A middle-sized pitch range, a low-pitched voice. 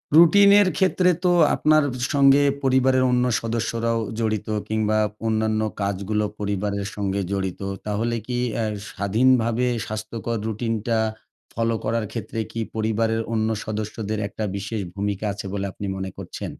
No: narrow, 2.3 semitones; low, 110 Hz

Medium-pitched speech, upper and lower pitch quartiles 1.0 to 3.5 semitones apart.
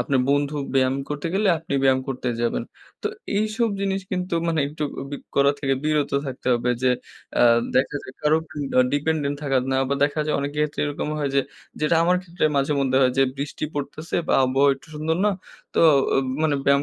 Yes: medium, 145 Hz; narrow, 2.5 semitones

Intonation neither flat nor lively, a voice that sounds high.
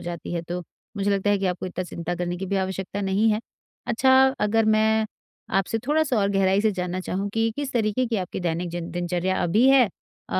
Yes: average, 3.5 semitones; high, 195 Hz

